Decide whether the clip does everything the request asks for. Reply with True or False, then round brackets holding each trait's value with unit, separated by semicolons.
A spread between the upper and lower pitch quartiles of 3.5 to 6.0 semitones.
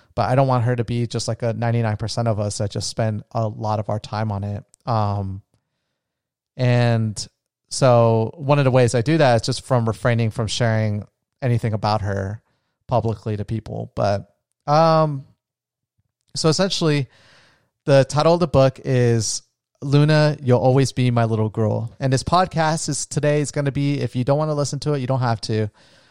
True (3.8 semitones)